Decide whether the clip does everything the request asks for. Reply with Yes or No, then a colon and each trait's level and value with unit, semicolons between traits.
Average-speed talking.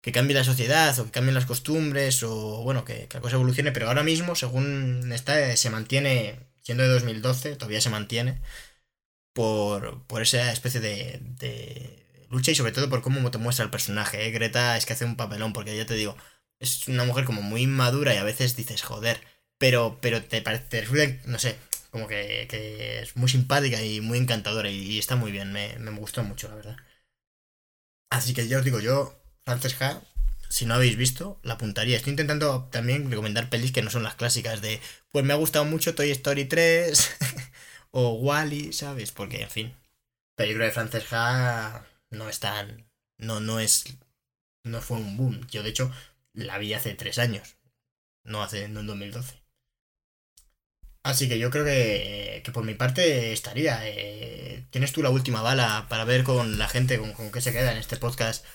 No: fast, 195 wpm